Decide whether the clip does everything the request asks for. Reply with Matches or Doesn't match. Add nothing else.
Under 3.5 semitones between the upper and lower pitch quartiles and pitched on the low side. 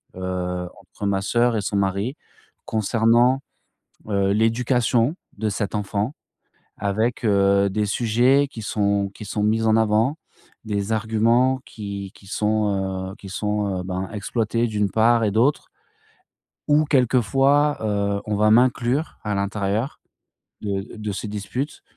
Matches